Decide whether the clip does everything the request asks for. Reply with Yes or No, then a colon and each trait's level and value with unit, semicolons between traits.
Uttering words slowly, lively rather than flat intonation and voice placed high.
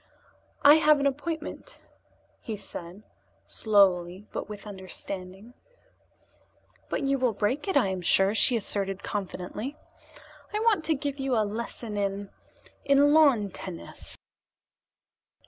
Yes: slow, 125 wpm; wide, 6.4 semitones; high, 215 Hz